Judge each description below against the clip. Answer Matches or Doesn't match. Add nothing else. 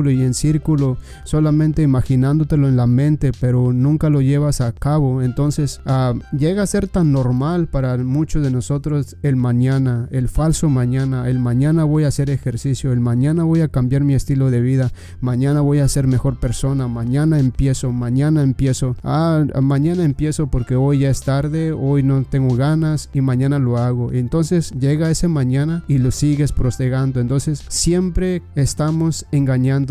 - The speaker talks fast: Doesn't match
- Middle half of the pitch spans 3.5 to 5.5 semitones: Doesn't match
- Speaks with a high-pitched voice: Doesn't match